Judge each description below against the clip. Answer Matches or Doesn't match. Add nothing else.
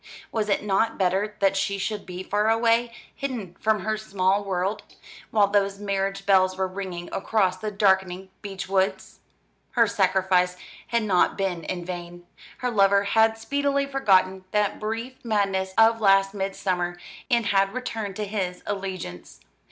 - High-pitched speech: Matches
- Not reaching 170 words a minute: Matches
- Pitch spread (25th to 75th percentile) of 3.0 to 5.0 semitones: Doesn't match